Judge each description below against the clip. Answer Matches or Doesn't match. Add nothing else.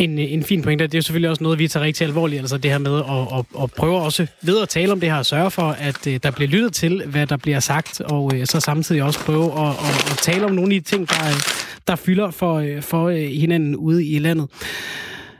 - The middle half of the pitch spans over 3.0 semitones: Doesn't match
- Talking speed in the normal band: Doesn't match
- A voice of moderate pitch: Matches